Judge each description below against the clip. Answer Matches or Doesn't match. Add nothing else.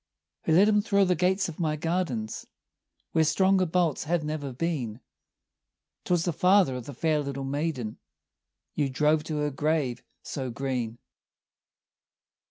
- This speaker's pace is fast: Doesn't match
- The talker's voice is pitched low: Doesn't match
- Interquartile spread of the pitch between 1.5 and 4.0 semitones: Doesn't match